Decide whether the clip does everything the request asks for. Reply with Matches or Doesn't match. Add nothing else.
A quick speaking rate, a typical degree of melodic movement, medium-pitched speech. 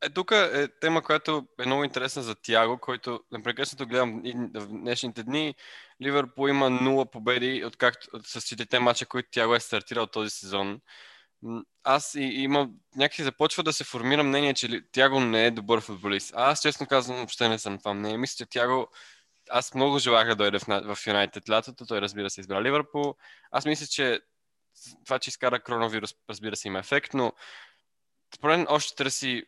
Doesn't match